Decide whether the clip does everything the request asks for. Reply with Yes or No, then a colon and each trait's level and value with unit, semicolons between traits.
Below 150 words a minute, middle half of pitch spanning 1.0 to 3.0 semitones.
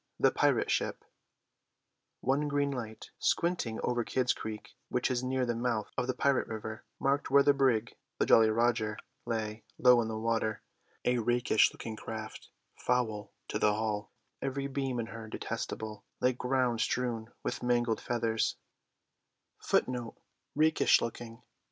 Yes: average, 140 wpm; narrow, 2.6 semitones